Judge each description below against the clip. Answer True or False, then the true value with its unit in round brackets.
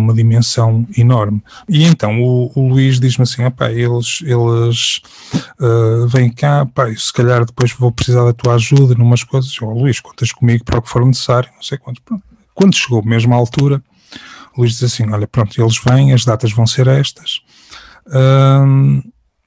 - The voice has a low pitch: True (125 Hz)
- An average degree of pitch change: False (2.3 semitones)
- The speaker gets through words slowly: False (180 wpm)